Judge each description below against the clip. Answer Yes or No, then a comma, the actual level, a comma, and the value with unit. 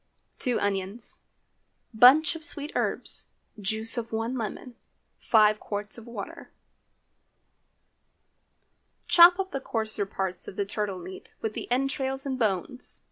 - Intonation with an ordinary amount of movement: Yes, average, 4.5 semitones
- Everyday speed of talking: No, slow, 130 wpm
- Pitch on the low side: No, high, 225 Hz